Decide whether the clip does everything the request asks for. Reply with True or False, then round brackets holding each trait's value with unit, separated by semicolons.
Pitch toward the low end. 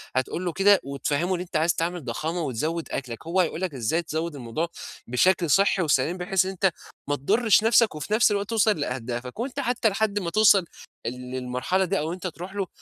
False (175 Hz)